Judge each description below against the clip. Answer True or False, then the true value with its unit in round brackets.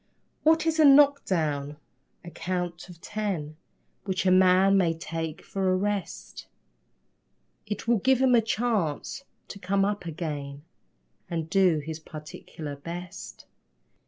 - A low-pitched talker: False (185 Hz)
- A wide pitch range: False (4.3 semitones)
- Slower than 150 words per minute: True (135 wpm)